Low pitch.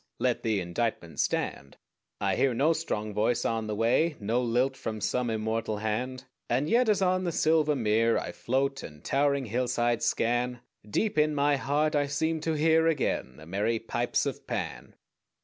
Yes: low, 125 Hz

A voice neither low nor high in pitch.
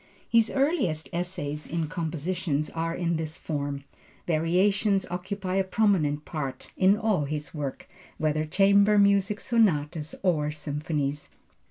Yes: medium, 165 Hz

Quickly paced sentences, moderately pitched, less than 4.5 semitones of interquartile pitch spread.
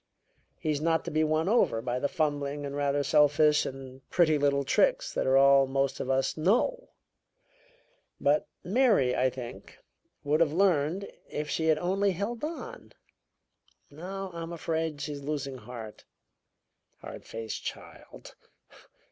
No: average, 140 wpm; medium, 150 Hz; average, 3.6 semitones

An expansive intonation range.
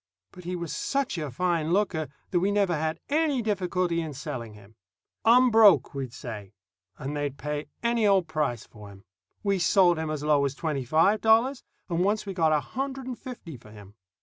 Yes: wide, 6.1 semitones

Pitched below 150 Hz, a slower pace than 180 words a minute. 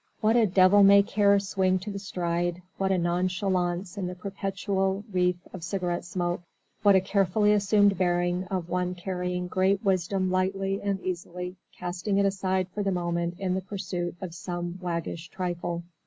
No: medium, 185 Hz; average, 170 wpm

